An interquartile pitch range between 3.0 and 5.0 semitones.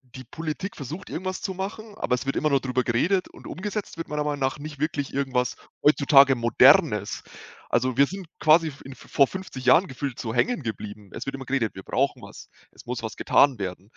Yes: average, 4.5 semitones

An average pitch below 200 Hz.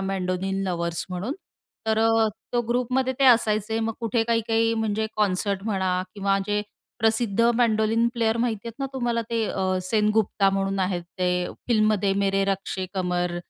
No: high, 210 Hz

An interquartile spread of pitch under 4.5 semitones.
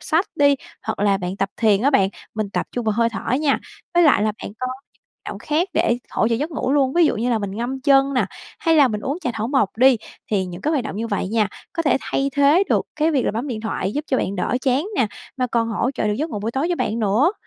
No: average, 5.0 semitones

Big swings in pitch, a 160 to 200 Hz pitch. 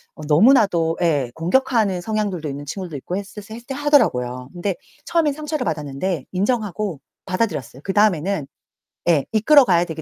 Yes: wide, 6.1 semitones; medium, 185 Hz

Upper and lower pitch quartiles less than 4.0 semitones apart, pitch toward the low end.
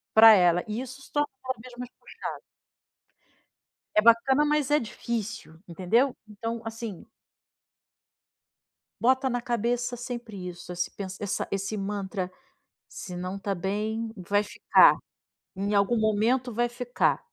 No: average, 3.6 semitones; high, 220 Hz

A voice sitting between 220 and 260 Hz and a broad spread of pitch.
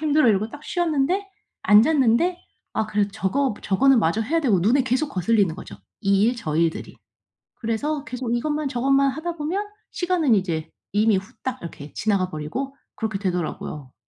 Yes: high, 230 Hz; wide, 6.8 semitones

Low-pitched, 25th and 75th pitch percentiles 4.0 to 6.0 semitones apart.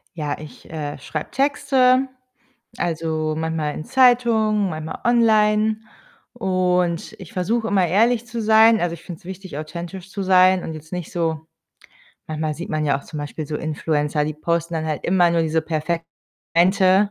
No: medium, 175 Hz; average, 5.1 semitones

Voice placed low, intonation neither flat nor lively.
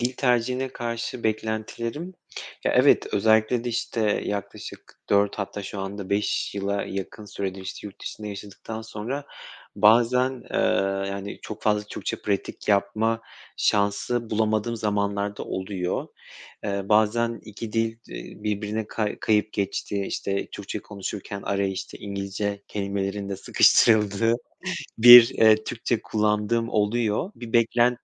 No: low, 105 Hz; narrow, 2.2 semitones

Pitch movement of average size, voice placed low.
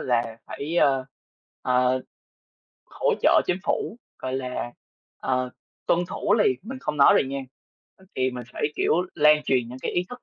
Yes: average, 4.1 semitones; low, 130 Hz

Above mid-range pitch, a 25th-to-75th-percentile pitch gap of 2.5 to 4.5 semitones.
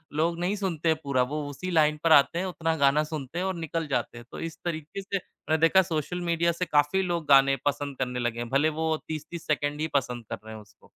No: medium, 155 Hz; average, 3.4 semitones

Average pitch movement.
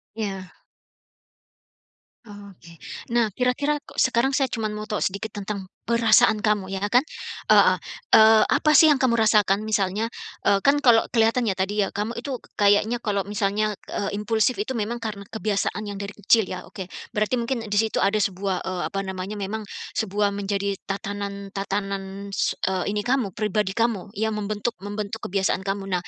No: narrow, 2.2 semitones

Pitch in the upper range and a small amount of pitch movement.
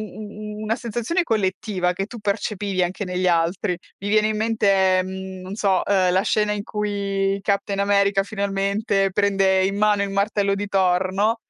Yes: high, 200 Hz; narrow, 1.7 semitones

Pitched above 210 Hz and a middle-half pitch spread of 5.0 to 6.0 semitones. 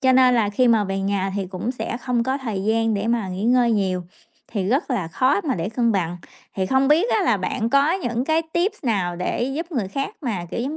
Yes: high, 235 Hz; average, 5.3 semitones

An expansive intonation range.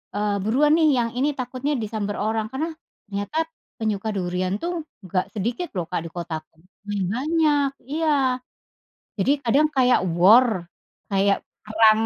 Yes: wide, 6.2 semitones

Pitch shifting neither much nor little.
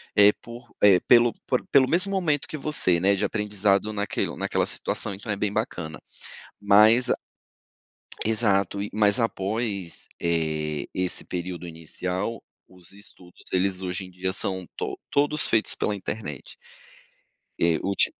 Yes: average, 3.6 semitones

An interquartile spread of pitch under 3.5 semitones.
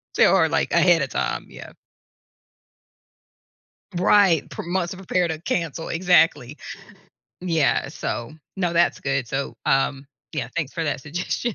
No: average, 4.3 semitones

